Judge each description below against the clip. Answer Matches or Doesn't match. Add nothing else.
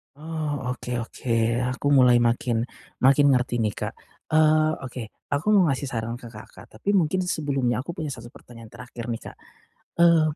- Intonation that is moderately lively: Matches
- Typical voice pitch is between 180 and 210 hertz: Doesn't match